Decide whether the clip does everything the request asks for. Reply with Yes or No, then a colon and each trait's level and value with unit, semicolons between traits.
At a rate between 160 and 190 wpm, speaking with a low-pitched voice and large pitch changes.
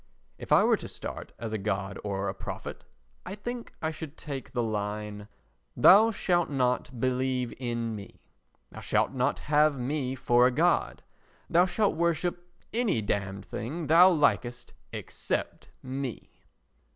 No: average, 150 wpm; low, 130 Hz; wide, 6.5 semitones